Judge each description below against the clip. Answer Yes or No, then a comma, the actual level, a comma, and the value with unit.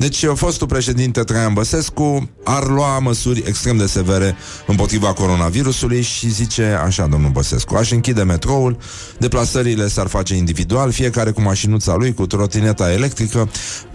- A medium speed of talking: Yes, average, 140 wpm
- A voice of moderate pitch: No, low, 115 Hz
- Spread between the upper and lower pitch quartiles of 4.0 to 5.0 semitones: Yes, average, 4.3 semitones